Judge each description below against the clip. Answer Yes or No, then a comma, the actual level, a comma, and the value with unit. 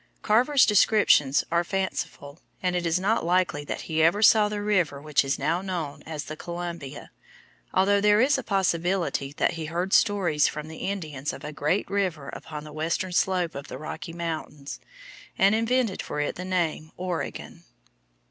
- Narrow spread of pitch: No, average, 4.2 semitones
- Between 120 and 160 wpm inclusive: No, average, 175 wpm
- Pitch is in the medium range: Yes, medium, 175 Hz